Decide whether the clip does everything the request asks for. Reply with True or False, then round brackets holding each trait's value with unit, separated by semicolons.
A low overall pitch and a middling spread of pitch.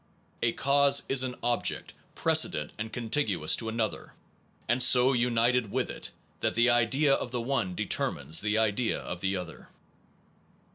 True (120 Hz; 3.1 semitones)